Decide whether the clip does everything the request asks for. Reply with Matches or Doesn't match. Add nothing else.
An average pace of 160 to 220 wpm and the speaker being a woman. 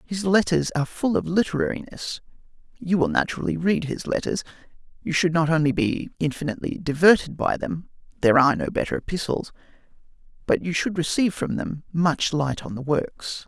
Doesn't match